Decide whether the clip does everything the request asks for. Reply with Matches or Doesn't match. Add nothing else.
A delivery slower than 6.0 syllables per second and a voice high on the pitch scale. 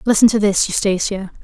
Matches